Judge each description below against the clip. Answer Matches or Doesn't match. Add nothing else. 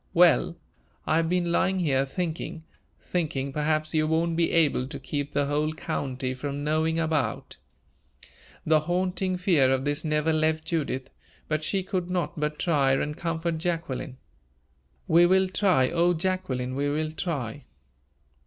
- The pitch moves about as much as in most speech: Matches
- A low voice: Doesn't match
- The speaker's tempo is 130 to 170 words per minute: Matches